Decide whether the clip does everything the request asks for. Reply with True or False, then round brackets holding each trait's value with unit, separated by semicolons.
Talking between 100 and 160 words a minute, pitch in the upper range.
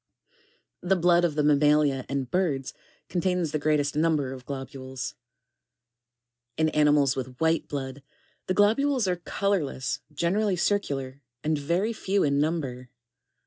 False (140 wpm; 150 Hz)